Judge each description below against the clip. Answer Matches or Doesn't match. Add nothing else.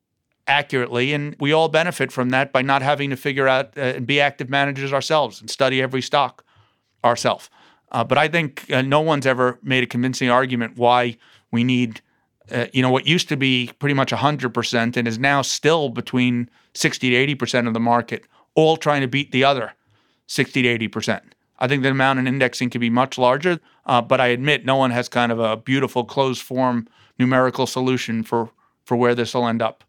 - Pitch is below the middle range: Matches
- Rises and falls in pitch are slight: Matches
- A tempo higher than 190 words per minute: Matches